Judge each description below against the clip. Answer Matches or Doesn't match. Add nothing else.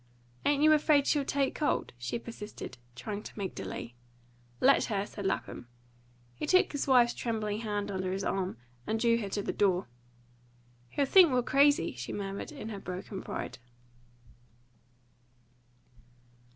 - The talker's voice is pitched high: Matches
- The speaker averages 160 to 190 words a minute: Doesn't match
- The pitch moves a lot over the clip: Matches